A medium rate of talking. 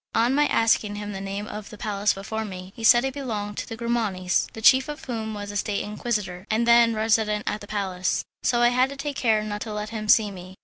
No: fast, 250 wpm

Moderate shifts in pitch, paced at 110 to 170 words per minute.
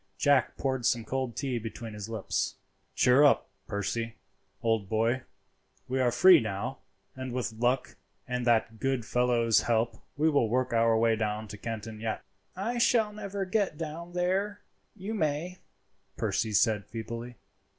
Yes: average, 5.0 semitones; average, 150 wpm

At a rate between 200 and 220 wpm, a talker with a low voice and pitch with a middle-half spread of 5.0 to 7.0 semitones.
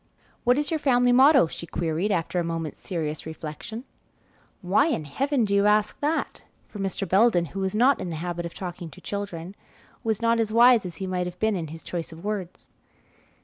No: fast, 205 wpm; high, 195 Hz; average, 5.3 semitones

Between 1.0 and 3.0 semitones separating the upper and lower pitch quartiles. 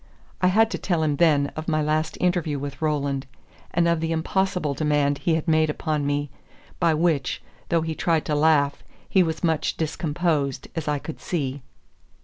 Yes: narrow, 2.4 semitones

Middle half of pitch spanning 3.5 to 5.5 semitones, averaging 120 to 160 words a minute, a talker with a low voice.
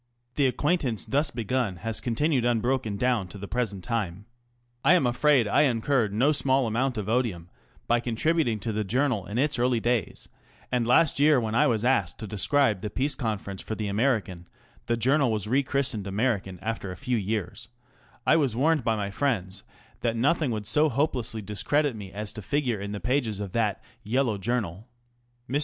No: average, 4.3 semitones; average, 190 wpm; low, 115 Hz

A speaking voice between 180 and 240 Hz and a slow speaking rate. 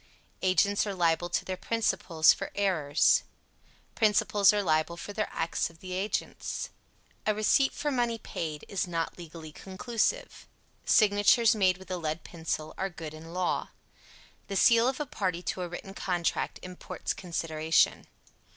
No: medium, 185 Hz; average, 150 wpm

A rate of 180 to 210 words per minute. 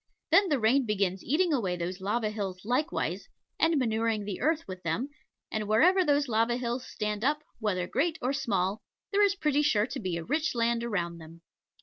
Yes: average, 190 wpm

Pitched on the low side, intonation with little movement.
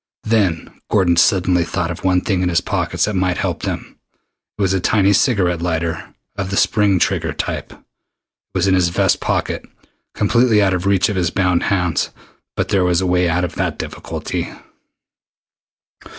Yes: very low, 90 Hz; narrow, 2.0 semitones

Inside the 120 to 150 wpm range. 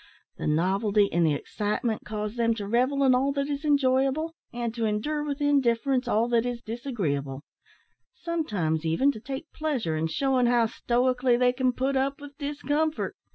No: average, 170 wpm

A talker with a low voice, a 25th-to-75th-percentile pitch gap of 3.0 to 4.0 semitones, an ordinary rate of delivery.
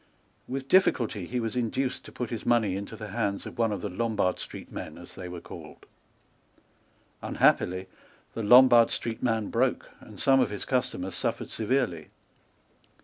Yes: low, 115 Hz; average, 3.7 semitones; average, 165 wpm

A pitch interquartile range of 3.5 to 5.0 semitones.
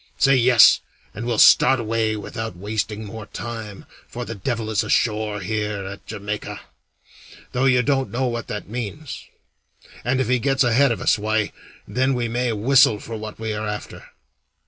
No: average, 2.8 semitones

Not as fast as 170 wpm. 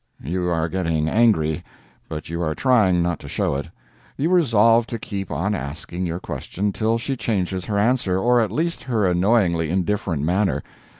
No: average, 175 wpm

